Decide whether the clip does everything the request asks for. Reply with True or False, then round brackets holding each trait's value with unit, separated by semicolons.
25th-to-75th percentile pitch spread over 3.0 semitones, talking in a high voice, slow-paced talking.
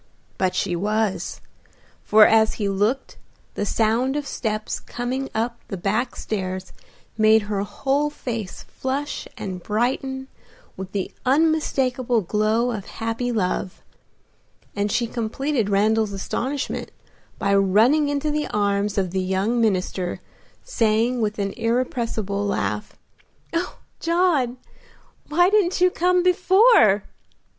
True (4.8 semitones; 225 Hz; 120 wpm)